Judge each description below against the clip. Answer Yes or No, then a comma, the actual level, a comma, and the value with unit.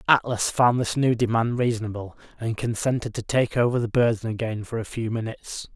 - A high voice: No, low, 115 Hz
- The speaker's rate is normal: Yes, average, 190 wpm